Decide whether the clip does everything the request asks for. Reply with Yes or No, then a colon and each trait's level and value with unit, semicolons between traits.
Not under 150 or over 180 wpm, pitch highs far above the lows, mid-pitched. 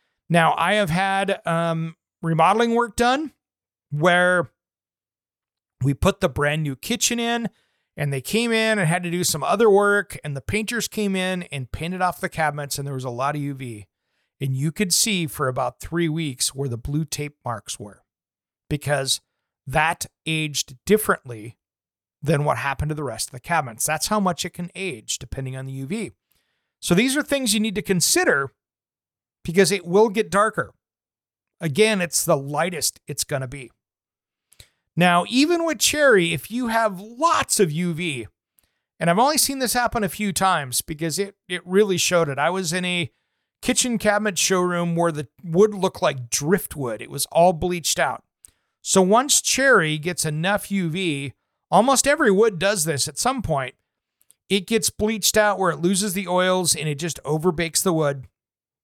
Yes: average, 175 wpm; wide, 5.9 semitones; medium, 175 Hz